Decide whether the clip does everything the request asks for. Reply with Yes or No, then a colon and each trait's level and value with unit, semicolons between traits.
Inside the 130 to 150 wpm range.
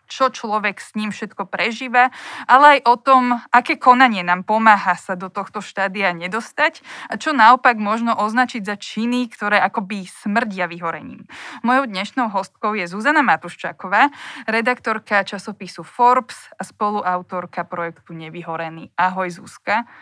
Yes: average, 135 wpm